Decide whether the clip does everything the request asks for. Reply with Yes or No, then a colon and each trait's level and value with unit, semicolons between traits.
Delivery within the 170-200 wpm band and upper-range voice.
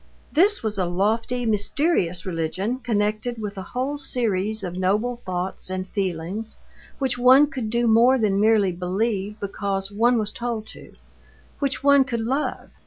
No: average, 155 wpm; high, 220 Hz